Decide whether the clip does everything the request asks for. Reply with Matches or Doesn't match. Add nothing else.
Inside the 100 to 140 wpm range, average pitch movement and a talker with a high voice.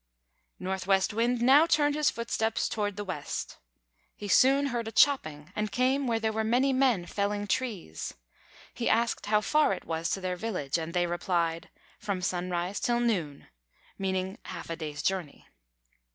Doesn't match